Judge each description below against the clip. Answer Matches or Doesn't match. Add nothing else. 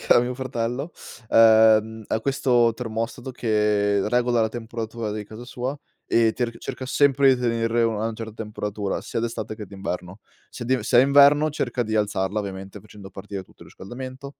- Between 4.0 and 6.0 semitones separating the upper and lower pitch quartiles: Doesn't match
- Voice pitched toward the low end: Matches